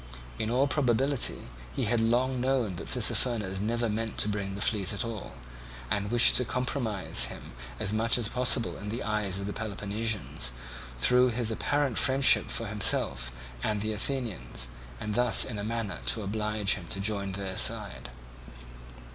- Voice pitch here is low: Yes, low, 110 Hz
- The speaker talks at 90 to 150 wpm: No, average, 165 wpm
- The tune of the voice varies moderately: Yes, average, 3.1 semitones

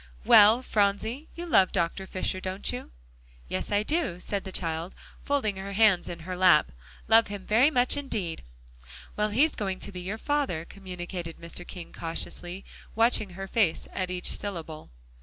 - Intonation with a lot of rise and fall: No, average, 3.7 semitones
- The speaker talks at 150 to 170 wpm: Yes, average, 165 wpm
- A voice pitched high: Yes, high, 195 Hz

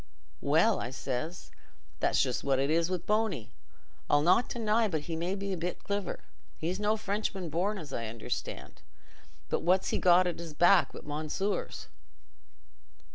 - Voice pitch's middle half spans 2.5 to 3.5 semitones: No, average, 5.0 semitones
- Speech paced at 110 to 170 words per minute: Yes, average, 150 wpm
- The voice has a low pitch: No, medium, 175 Hz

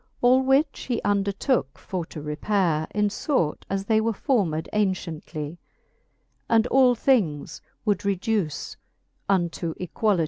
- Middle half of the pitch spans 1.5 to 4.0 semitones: No, wide, 5.5 semitones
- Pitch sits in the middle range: No, high, 200 Hz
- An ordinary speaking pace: No, slow, 125 wpm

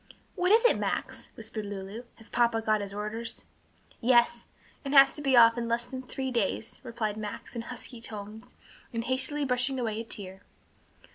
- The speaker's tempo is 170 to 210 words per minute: Yes, average, 180 wpm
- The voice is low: No, high, 235 Hz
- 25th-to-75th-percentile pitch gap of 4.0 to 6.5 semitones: No, average, 3.0 semitones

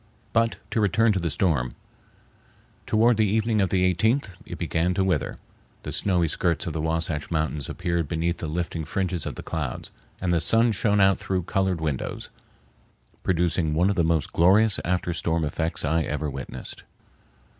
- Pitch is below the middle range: Yes, very low, 85 Hz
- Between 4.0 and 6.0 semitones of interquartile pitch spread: No, average, 3.3 semitones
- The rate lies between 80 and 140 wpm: No, average, 175 wpm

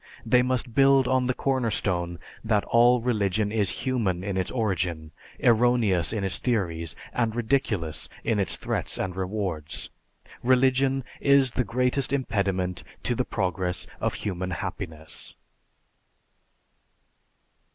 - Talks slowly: Yes, slow, 125 wpm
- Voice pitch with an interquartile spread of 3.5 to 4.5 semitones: No, wide, 5.5 semitones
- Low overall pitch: Yes, low, 110 Hz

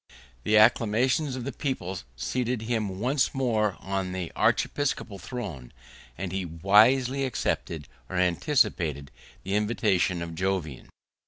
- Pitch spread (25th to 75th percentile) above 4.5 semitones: Yes, wide, 5.5 semitones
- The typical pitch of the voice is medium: No, low, 105 Hz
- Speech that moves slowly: Yes, slow, 120 wpm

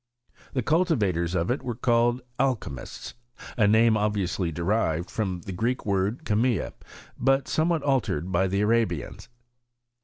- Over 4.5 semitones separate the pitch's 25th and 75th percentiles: Yes, average, 5.2 semitones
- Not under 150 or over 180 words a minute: No, average, 140 wpm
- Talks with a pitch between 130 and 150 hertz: No, low, 110 Hz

